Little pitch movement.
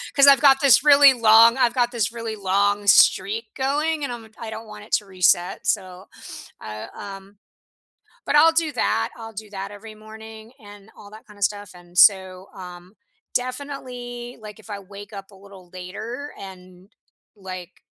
No: average, 3.9 semitones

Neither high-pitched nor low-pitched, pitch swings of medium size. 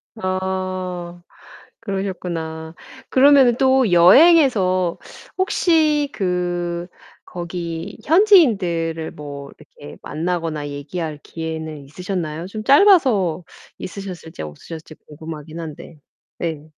Yes: medium, 175 Hz; average, 4.5 semitones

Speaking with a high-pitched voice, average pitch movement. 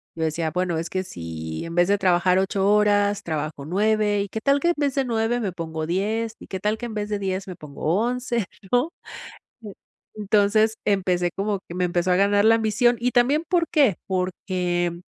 Yes: high, 200 Hz; average, 3.9 semitones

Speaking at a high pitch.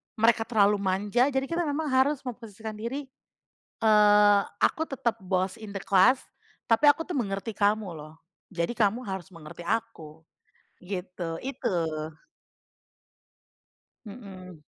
Yes: high, 210 Hz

